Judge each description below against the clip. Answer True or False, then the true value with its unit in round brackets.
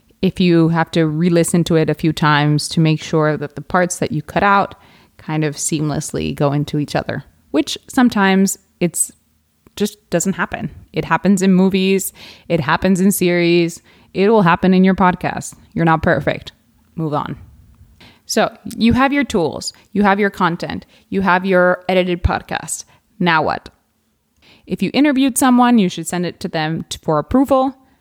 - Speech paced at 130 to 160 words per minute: False (175 wpm)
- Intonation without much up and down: False (3.8 semitones)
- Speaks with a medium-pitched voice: True (180 Hz)